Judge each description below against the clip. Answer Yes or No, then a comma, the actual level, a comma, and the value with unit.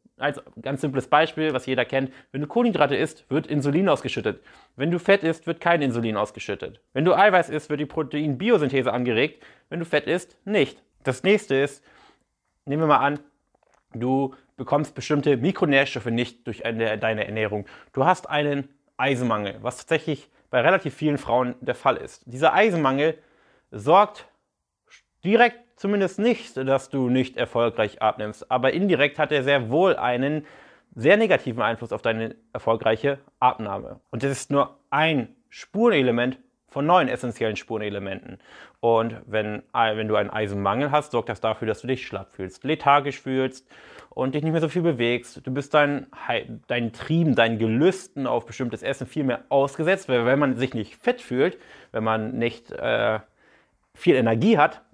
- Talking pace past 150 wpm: Yes, average, 165 wpm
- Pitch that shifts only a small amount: No, average, 4.3 semitones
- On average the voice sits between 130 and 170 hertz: Yes, low, 135 Hz